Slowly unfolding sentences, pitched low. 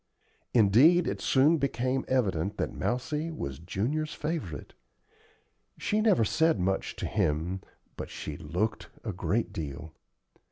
Yes: slow, 125 wpm; low, 115 Hz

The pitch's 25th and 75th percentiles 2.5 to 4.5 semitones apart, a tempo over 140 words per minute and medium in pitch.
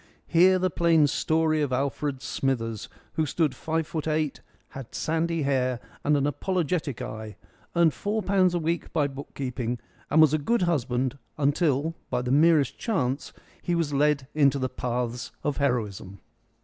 Yes: average, 3.9 semitones; average, 160 wpm; medium, 145 Hz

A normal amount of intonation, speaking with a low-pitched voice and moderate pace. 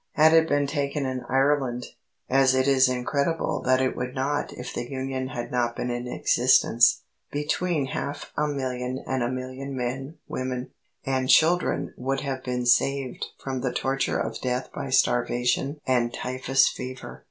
No: narrow, 1.7 semitones; low, 130 Hz; average, 165 wpm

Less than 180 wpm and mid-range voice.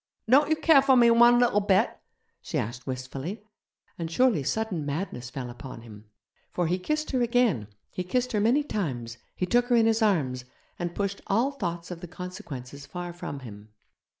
No: average, 185 wpm; medium, 180 Hz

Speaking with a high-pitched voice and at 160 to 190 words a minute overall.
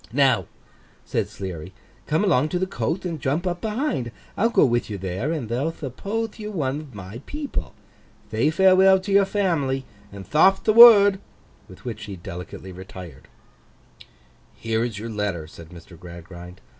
No: low, 130 Hz; average, 165 wpm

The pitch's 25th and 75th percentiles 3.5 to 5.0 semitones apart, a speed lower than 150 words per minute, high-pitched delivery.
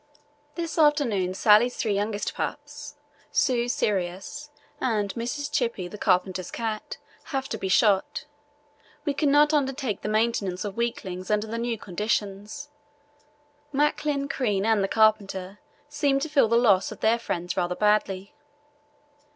No: wide, 5.4 semitones; average, 140 wpm; high, 220 Hz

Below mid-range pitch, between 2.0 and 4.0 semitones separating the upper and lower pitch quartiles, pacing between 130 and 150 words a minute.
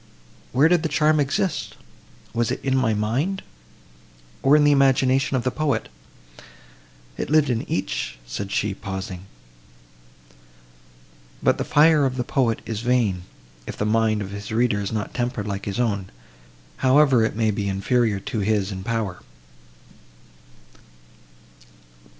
No: low, 115 Hz; average, 4.8 semitones; average, 140 wpm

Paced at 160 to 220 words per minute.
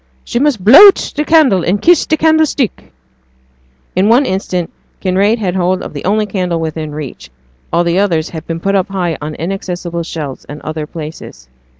Yes: average, 185 wpm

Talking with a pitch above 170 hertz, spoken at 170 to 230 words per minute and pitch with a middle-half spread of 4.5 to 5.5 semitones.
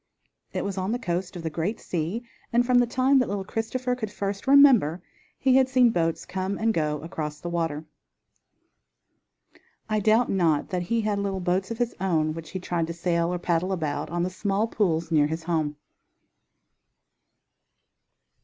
Yes: medium, 185 Hz; average, 180 wpm; average, 5.2 semitones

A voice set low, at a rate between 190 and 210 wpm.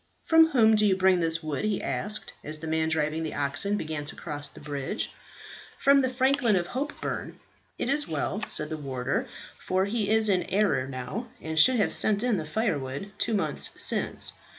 No: medium, 185 Hz; average, 195 wpm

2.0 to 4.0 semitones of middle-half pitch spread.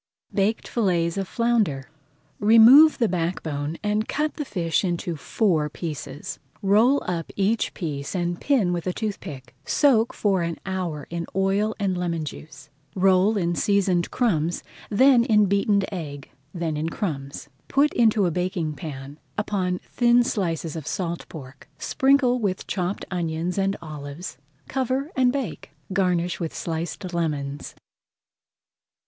No: average, 4.6 semitones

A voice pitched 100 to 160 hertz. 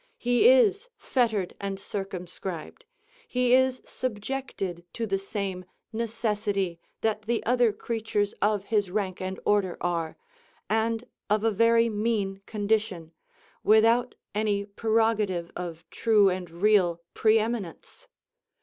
No: high, 210 Hz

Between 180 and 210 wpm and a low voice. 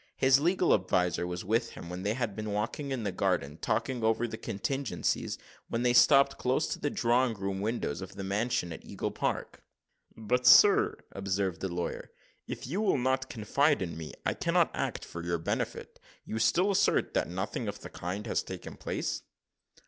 Yes: average, 185 wpm; low, 110 Hz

